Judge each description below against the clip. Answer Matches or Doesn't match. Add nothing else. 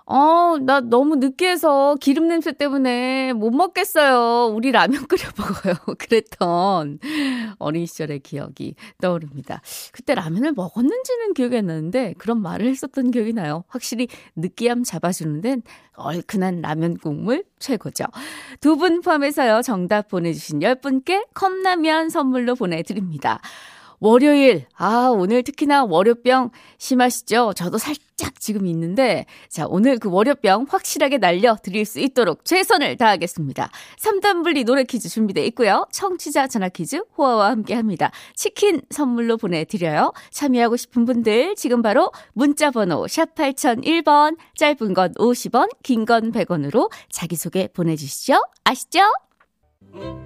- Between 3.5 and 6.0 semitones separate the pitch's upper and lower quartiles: Doesn't match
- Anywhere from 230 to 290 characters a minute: Doesn't match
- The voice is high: Matches